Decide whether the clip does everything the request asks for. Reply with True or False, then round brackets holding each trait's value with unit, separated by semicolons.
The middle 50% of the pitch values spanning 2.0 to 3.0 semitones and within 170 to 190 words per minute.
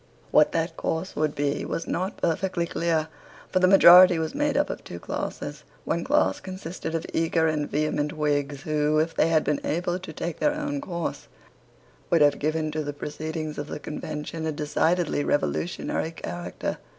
True (2.5 semitones; 175 wpm)